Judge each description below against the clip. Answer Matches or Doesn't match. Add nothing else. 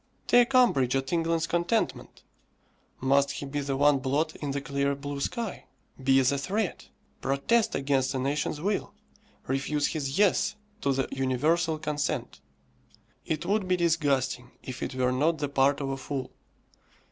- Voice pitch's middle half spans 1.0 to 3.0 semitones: Doesn't match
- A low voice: Doesn't match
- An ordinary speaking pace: Matches